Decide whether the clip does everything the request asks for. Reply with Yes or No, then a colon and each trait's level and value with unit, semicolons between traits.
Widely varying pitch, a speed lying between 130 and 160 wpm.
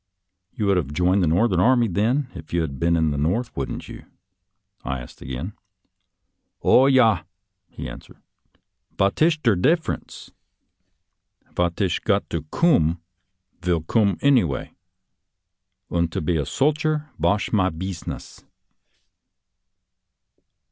Yes: wide, 6.5 semitones; average, 140 wpm